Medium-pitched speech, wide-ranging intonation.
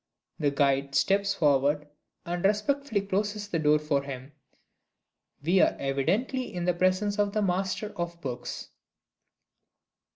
Yes: medium, 175 Hz; wide, 5.9 semitones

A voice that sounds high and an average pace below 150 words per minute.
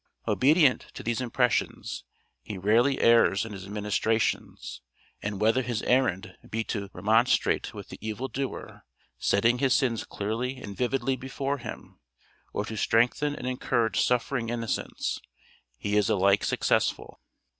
No: low, 115 Hz; slow, 135 wpm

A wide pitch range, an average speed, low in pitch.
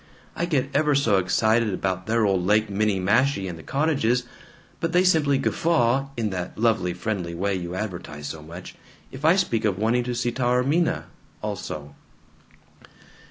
Yes: wide, 6.5 semitones; average, 160 wpm; low, 110 Hz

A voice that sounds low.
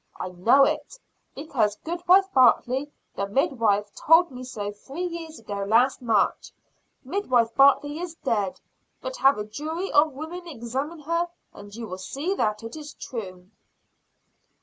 No: very high, 270 Hz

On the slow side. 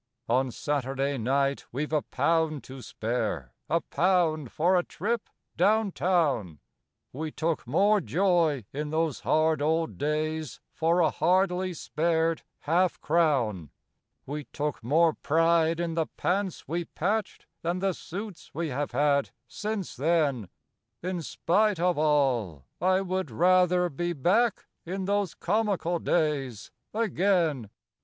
Yes: slow, 130 wpm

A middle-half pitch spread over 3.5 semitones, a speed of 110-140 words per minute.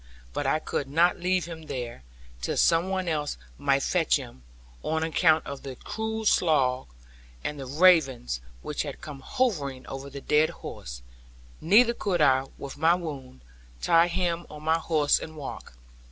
No: average, 4.1 semitones; average, 165 wpm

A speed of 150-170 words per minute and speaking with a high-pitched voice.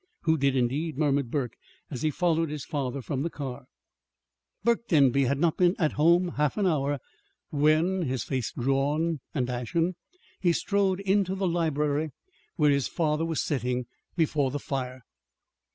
No: average, 160 wpm; medium, 150 Hz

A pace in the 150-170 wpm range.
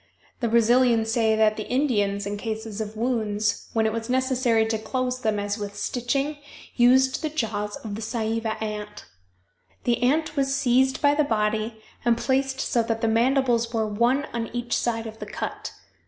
No: average, 180 wpm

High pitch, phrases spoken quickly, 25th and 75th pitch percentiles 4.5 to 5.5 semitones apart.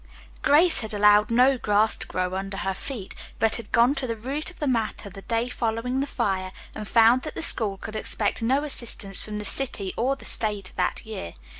No: high, 225 Hz; fast, 210 wpm; average, 3.8 semitones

